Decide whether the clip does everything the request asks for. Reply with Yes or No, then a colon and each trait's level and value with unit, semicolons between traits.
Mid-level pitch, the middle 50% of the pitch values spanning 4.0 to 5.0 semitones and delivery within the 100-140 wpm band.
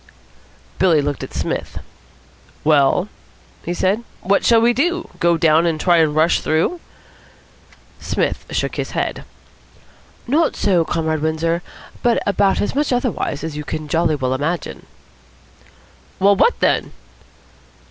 Yes: medium, 170 Hz; average, 4.7 semitones; slow, 135 wpm